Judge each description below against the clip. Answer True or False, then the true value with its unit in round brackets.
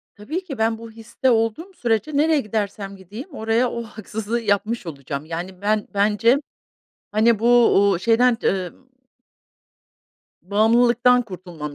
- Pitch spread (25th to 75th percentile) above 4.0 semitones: False (3.1 semitones)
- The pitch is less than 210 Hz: False (220 Hz)